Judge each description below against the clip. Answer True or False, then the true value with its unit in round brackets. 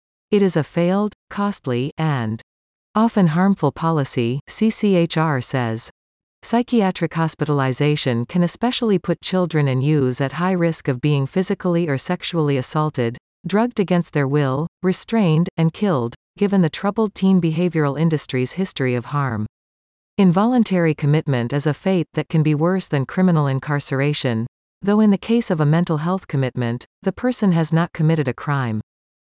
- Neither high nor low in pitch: True (160 Hz)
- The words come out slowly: False (150 wpm)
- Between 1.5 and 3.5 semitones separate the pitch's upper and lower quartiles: False (5.3 semitones)